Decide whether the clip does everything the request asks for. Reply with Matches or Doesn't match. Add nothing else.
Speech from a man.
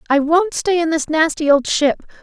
Doesn't match